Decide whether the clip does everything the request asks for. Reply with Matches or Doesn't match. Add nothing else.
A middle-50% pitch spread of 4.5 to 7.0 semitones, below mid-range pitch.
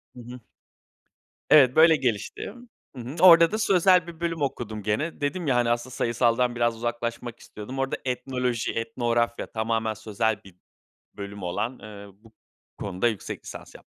Doesn't match